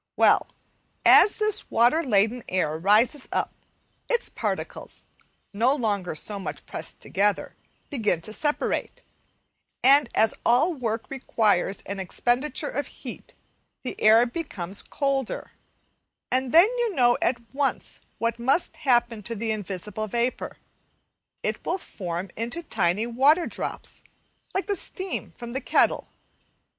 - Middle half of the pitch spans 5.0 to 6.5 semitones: Yes, wide, 5.4 semitones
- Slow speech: Yes, slow, 130 wpm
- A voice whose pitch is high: Yes, high, 240 Hz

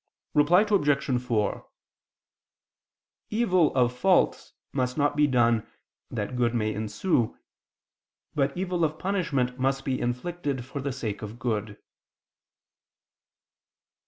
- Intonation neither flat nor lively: Yes, average, 4.5 semitones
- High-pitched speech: No, low, 135 Hz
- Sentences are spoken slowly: Yes, slow, 110 wpm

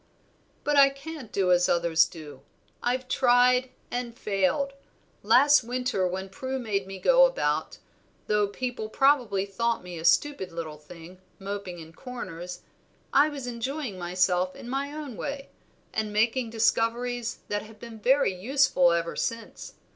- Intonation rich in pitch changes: Yes, wide, 6.0 semitones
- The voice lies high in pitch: Yes, high, 225 Hz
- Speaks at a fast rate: No, average, 145 wpm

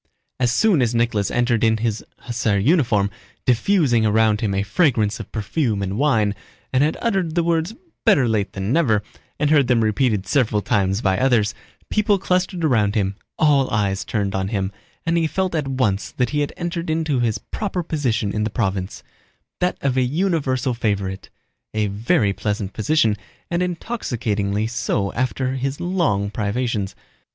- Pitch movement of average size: No, wide, 6.7 semitones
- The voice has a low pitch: Yes, low, 120 Hz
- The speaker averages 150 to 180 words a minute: Yes, average, 165 wpm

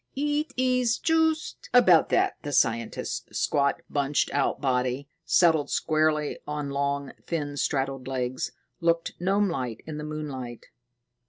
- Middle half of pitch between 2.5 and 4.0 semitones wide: No, average, 4.4 semitones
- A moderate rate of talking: No, slow, 120 wpm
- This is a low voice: No, medium, 150 Hz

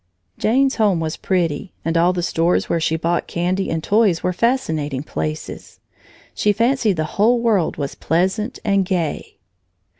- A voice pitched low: No, medium, 180 Hz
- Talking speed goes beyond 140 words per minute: Yes, average, 155 wpm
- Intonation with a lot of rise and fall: No, average, 4.7 semitones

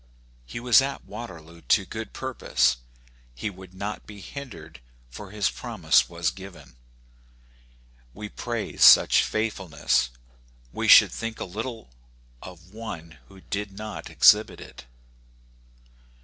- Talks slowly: Yes, slow, 120 wpm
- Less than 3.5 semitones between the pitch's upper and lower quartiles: No, average, 4.6 semitones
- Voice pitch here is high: No, low, 100 Hz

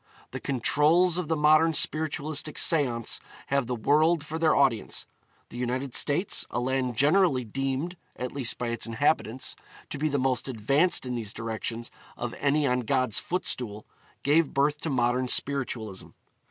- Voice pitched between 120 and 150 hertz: Yes, low, 135 Hz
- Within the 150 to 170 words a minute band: Yes, average, 155 wpm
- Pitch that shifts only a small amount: No, average, 3.9 semitones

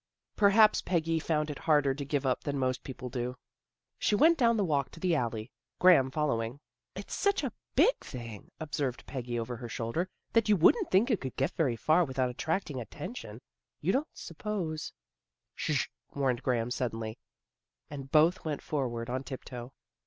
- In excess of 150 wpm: Yes, average, 180 wpm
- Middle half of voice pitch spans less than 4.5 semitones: No, wide, 5.4 semitones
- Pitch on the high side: No, medium, 140 Hz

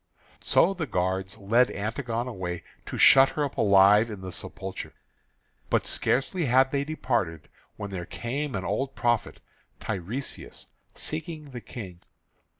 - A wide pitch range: Yes, wide, 6.0 semitones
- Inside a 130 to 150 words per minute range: Yes, average, 140 wpm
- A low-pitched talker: Yes, low, 115 Hz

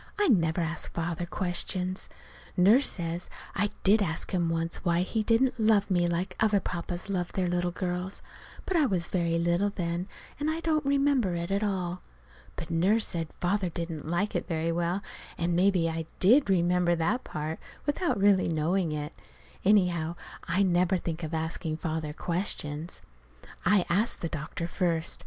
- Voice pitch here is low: No, medium, 175 Hz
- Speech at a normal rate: Yes, average, 165 wpm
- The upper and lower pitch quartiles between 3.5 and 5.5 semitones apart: No, average, 3.0 semitones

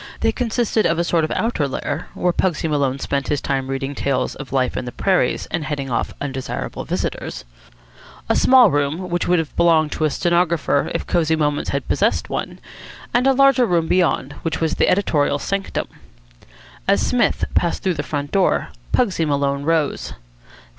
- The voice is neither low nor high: Yes, medium, 160 Hz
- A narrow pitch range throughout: No, average, 4.3 semitones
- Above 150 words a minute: Yes, average, 180 wpm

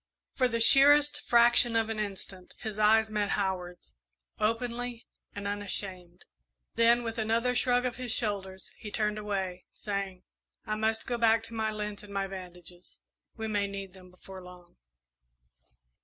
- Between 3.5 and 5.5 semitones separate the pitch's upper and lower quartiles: No, average, 3.1 semitones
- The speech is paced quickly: No, average, 155 wpm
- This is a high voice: Yes, high, 210 Hz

